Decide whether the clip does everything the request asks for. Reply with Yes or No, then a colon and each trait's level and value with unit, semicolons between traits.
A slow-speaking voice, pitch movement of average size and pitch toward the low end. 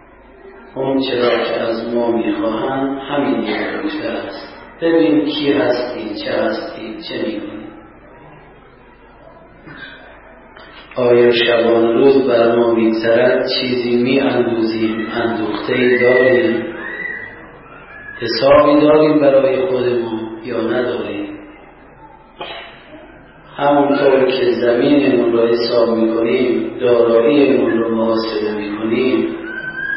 Yes: slow, 80 wpm; average, 3.6 semitones; low, 120 Hz